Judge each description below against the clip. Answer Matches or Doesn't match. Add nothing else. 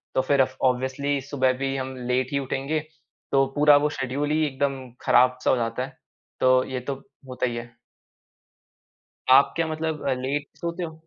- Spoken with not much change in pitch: Matches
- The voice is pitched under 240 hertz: Matches